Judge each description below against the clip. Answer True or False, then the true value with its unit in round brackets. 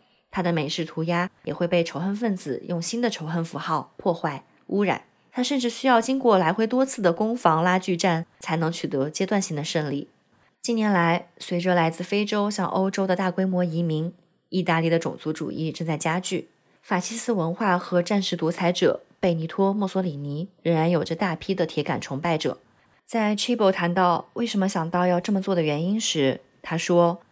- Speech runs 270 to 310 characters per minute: True (295 characters per minute)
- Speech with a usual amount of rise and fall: True (3.1 semitones)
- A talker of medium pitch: True (175 Hz)